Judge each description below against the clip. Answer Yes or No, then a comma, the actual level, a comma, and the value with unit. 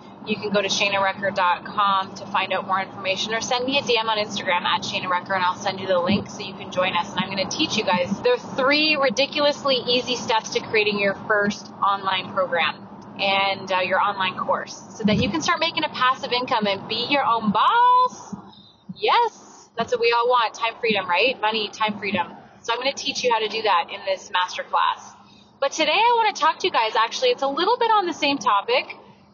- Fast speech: Yes, fast, 225 wpm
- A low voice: No, high, 220 Hz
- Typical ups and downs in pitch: No, wide, 6.0 semitones